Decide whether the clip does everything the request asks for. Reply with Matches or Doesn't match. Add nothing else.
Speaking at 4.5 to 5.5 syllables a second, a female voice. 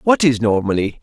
Doesn't match